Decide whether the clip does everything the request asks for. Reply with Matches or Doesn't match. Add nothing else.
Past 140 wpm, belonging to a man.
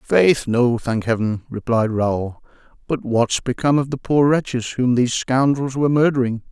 Matches